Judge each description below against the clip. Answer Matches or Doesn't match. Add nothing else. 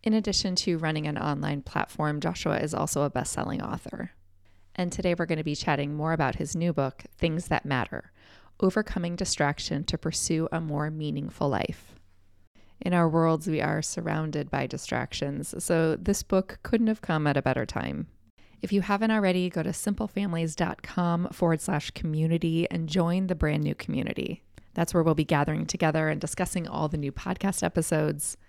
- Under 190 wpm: Matches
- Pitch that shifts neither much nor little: Matches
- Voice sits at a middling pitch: Matches